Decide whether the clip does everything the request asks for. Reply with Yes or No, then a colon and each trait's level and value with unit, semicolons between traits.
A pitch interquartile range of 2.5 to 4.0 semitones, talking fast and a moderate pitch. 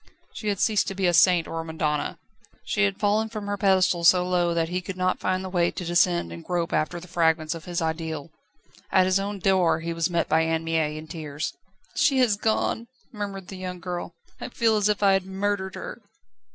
Yes: average, 3.1 semitones; fast, 225 wpm; medium, 180 Hz